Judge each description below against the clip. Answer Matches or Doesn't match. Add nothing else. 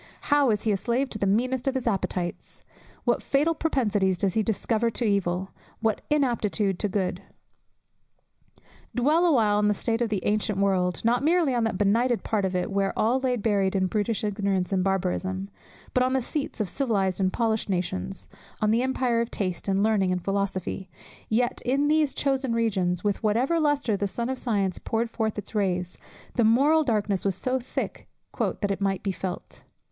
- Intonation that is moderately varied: Matches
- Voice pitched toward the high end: Matches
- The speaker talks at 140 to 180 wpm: Doesn't match